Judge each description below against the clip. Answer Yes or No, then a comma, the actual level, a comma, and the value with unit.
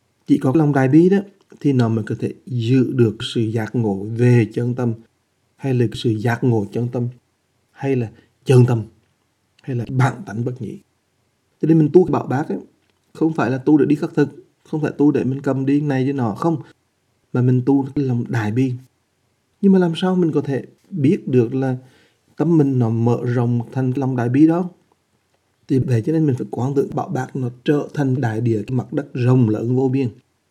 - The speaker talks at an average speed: No, fast, 220 wpm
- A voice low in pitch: Yes, low, 130 Hz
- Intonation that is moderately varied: Yes, average, 3.4 semitones